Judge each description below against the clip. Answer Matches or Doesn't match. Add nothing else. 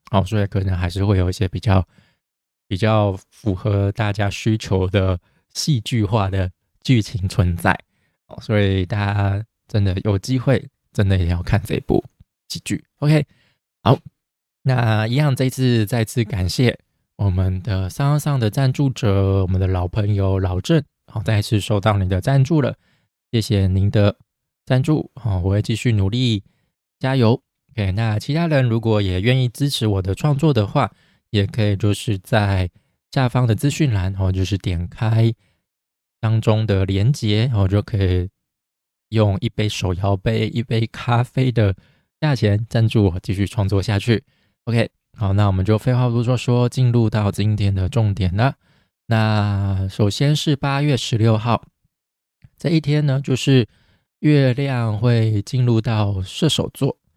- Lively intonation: Doesn't match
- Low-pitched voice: Matches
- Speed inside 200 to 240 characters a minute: Matches